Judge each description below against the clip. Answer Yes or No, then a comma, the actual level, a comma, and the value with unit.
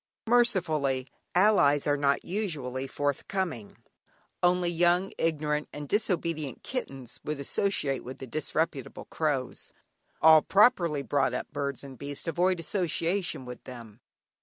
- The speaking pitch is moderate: Yes, medium, 150 Hz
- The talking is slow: Yes, slow, 120 wpm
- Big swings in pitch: No, average, 4.4 semitones